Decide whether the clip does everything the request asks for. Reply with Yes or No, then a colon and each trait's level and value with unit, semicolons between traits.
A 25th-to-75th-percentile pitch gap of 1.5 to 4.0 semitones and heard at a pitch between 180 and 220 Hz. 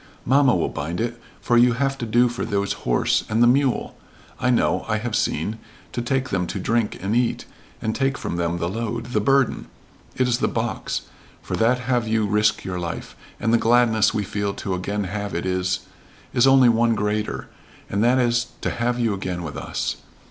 No: average, 3.4 semitones; low, 115 Hz